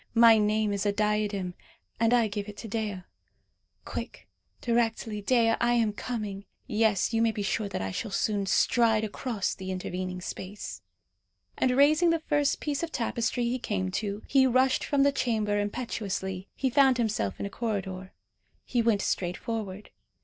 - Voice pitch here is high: Yes, high, 215 Hz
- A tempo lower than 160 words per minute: No, average, 170 wpm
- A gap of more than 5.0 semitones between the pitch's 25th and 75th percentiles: No, average, 3.1 semitones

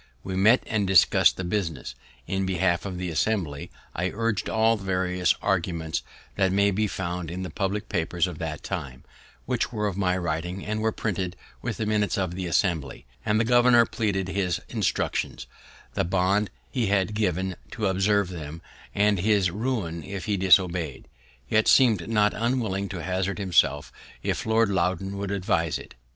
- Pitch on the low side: Yes, very low, 95 Hz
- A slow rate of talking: No, average, 170 wpm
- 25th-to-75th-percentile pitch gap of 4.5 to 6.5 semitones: No, average, 3.0 semitones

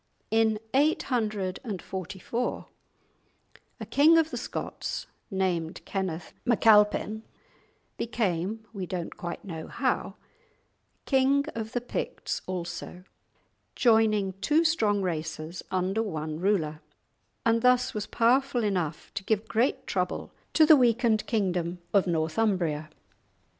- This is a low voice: No, high, 210 Hz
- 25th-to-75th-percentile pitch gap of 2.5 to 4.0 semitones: No, average, 4.7 semitones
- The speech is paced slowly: Yes, slow, 110 wpm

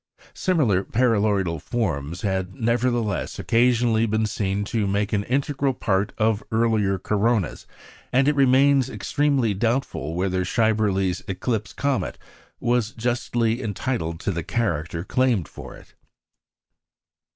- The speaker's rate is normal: No, slow, 120 wpm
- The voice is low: Yes, low, 110 Hz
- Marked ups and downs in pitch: No, average, 4.1 semitones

